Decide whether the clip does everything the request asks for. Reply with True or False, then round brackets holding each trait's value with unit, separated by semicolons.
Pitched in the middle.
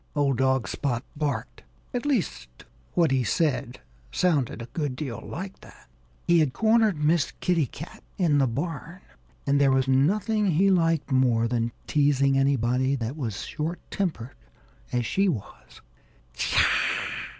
True (145 Hz)